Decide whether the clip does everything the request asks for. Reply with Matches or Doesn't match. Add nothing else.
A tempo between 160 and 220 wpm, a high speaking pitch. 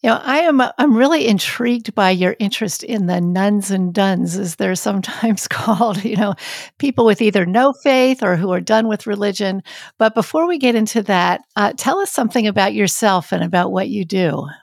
Matches